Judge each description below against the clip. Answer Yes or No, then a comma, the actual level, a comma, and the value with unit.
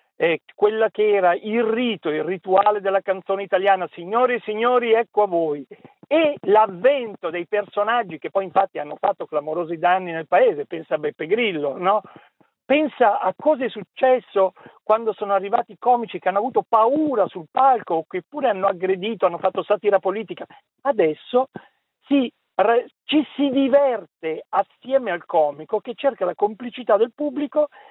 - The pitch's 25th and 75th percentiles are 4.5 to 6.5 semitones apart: Yes, average, 5.2 semitones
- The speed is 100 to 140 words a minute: No, average, 160 wpm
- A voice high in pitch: Yes, high, 210 Hz